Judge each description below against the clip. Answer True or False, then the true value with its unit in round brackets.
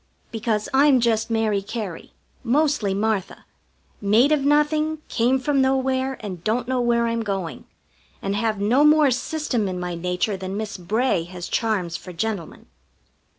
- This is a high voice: True (225 Hz)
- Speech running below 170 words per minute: True (150 wpm)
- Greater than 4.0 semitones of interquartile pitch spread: True (5.0 semitones)